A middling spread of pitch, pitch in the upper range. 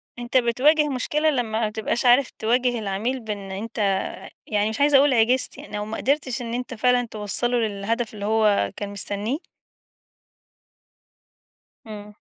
Yes: average, 3.1 semitones; high, 230 Hz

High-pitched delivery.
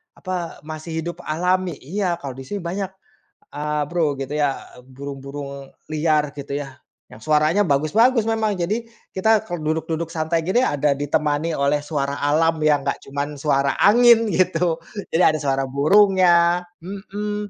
No: medium, 160 Hz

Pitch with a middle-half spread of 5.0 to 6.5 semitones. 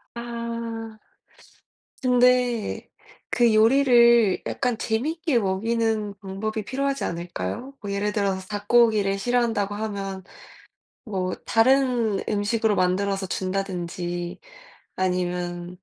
No: average, 3.7 semitones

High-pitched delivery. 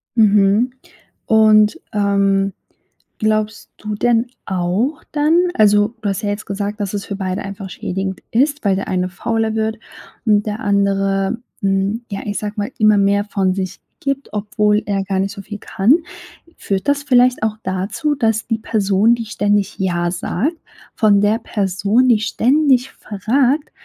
Yes: high, 210 Hz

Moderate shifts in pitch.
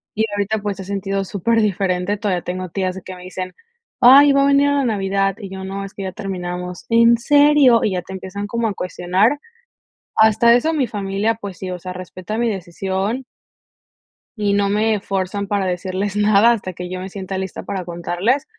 Yes: average, 3.1 semitones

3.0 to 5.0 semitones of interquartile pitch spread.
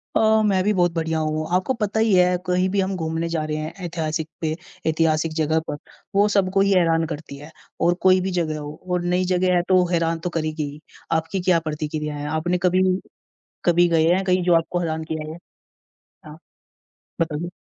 No: narrow, 2.6 semitones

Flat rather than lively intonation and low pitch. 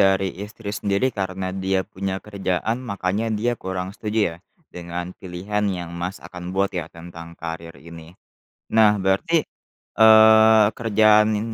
No: average, 3.3 semitones; very low, 95 Hz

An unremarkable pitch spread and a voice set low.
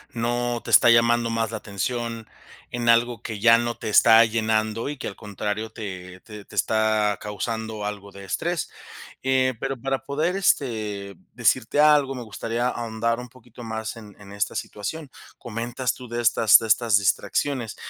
No: narrow, 2.2 semitones; low, 115 Hz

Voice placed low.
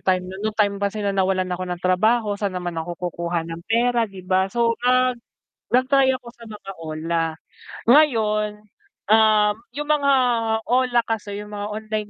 No: high, 210 Hz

